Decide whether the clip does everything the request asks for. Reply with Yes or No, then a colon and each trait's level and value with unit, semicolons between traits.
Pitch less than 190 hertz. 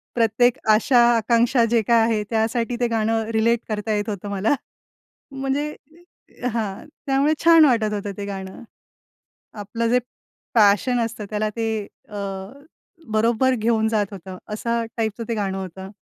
No: high, 225 Hz